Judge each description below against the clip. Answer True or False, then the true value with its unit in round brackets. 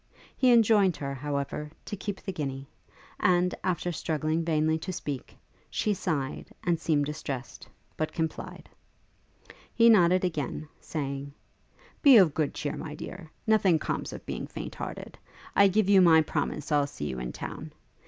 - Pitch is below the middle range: False (160 Hz)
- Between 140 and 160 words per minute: True (155 wpm)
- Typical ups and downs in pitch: True (4.3 semitones)